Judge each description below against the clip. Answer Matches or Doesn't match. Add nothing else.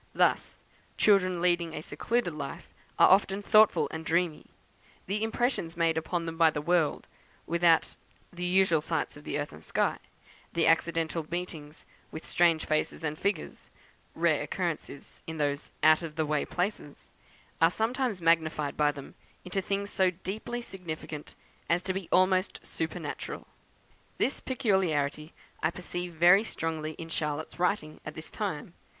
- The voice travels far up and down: Doesn't match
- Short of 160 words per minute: Matches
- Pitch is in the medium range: Matches